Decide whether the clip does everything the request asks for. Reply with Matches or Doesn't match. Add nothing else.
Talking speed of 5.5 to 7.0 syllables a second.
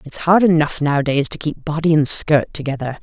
Matches